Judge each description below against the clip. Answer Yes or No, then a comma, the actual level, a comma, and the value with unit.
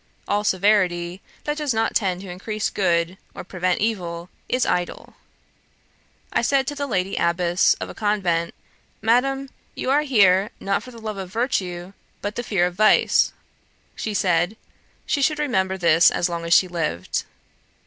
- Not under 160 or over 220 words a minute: Yes, average, 165 wpm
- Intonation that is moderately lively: Yes, average, 4.2 semitones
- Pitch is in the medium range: No, high, 195 Hz